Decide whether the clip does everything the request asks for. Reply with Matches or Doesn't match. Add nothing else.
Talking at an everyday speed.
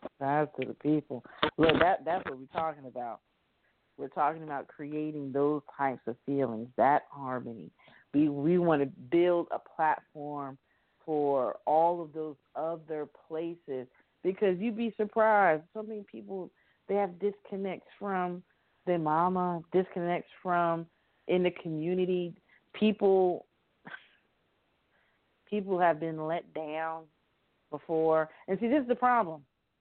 Doesn't match